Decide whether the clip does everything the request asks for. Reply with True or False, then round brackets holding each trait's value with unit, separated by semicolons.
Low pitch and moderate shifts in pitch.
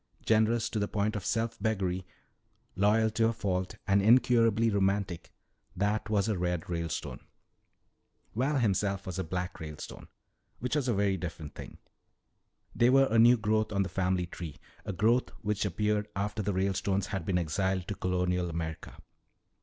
True (100 Hz; 3.2 semitones)